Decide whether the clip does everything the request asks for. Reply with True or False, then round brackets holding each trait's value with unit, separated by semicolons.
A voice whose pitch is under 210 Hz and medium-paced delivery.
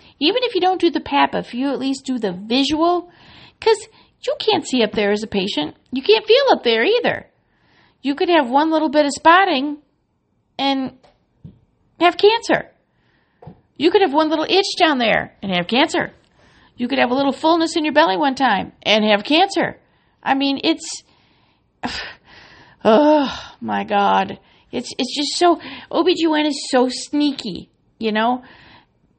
False (290 Hz; 165 wpm)